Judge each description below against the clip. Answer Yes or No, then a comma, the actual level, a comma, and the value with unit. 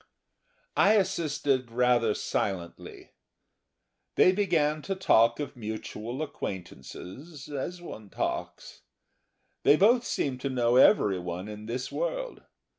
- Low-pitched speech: Yes, low, 130 Hz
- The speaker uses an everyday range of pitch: No, wide, 7.9 semitones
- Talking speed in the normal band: No, slow, 110 wpm